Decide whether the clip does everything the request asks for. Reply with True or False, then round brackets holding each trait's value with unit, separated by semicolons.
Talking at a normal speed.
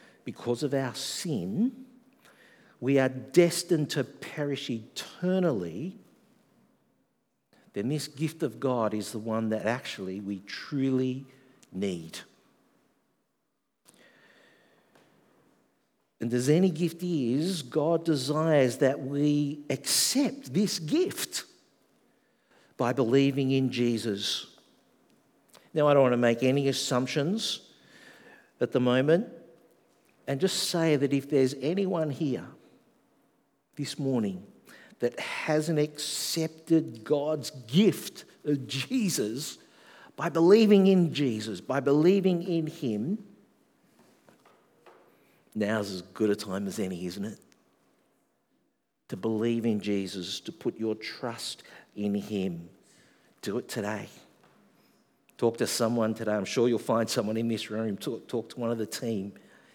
False (115 wpm)